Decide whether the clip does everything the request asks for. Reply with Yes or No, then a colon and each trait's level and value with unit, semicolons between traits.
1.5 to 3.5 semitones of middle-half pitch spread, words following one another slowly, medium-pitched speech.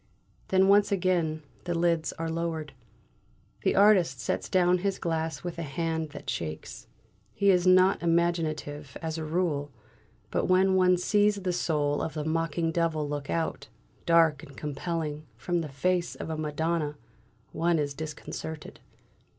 No: average, 2.7 semitones; average, 150 wpm; medium, 165 Hz